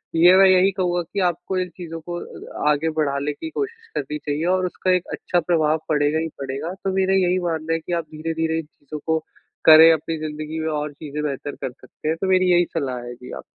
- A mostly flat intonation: No, average, 3.0 semitones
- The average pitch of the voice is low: No, medium, 160 Hz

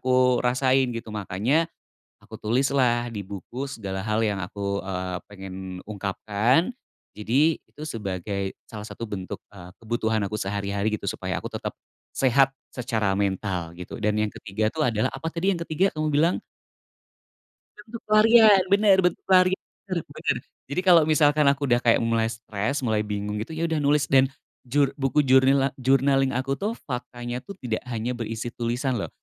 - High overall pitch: No, low, 120 Hz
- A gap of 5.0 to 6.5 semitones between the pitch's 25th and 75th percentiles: Yes, average, 5.3 semitones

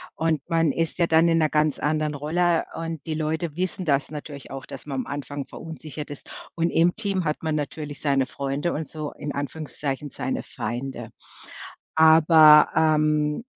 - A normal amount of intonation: No, narrow, 2.1 semitones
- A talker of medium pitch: Yes, medium, 155 Hz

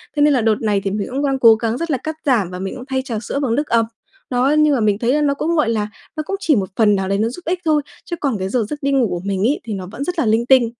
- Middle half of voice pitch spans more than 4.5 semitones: Yes, average, 5.2 semitones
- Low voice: No, high, 245 Hz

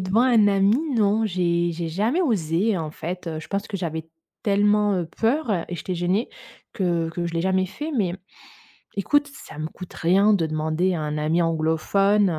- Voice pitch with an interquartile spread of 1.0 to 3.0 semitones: No, average, 3.8 semitones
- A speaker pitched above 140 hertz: Yes, medium, 185 Hz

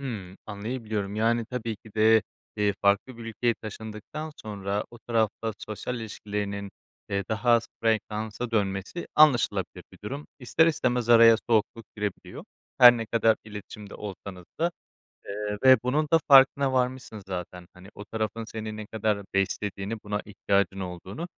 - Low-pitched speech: Yes, low, 110 Hz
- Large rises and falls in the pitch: No, average, 2.7 semitones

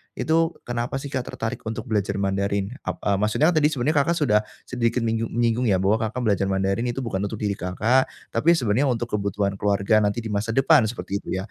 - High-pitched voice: No, low, 110 Hz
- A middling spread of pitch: Yes, average, 3.8 semitones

